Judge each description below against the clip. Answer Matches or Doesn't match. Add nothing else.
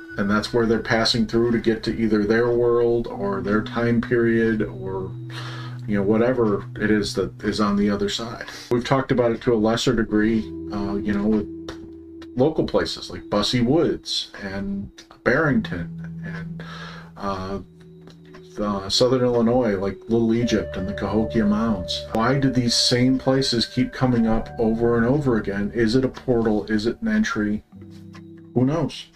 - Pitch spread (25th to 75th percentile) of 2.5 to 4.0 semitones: Matches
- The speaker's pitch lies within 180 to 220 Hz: Doesn't match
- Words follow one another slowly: Doesn't match